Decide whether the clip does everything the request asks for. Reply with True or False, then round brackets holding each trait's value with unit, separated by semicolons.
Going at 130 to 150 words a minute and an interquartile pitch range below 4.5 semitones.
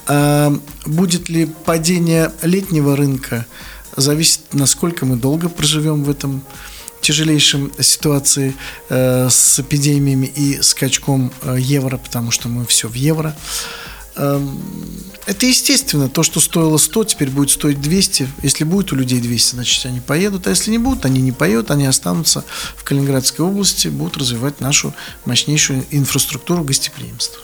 True (135 wpm; 3.4 semitones)